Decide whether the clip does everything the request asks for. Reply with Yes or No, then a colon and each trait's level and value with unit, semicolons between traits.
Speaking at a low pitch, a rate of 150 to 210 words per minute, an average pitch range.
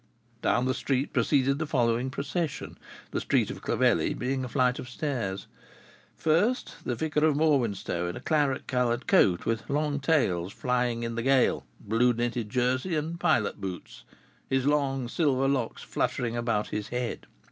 Yes: low, 130 Hz; average, 160 wpm; average, 3.4 semitones